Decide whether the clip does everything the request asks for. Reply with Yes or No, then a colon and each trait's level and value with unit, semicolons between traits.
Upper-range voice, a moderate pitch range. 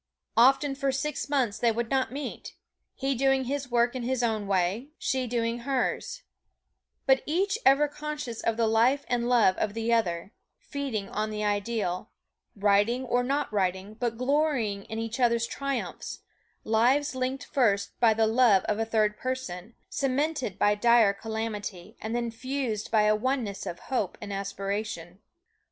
Yes: high, 235 Hz; average, 3.9 semitones